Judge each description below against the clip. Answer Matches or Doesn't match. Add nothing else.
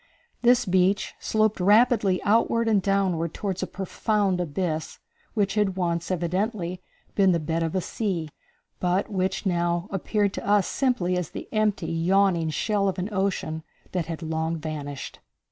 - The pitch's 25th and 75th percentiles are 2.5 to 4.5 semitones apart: Matches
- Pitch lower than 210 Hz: Matches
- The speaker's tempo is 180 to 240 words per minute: Doesn't match